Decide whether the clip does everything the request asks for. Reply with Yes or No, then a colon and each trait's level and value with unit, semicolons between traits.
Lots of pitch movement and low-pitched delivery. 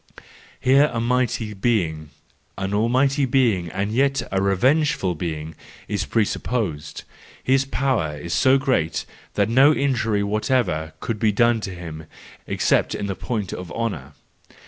Yes: wide, 6.2 semitones; low, 110 Hz